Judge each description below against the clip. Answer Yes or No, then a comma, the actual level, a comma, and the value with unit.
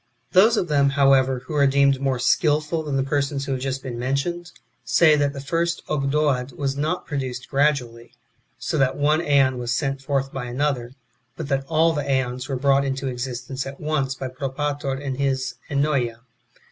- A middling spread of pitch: No, narrow, 1.9 semitones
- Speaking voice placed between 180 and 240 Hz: No, low, 135 Hz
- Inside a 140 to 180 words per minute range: No, average, 190 wpm